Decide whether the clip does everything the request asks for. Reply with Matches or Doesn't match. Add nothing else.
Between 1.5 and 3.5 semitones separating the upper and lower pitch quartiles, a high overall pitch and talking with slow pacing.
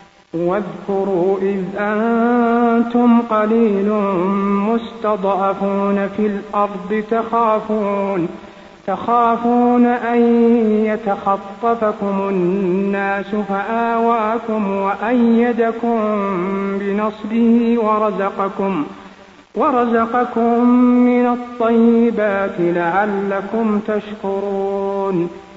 Matches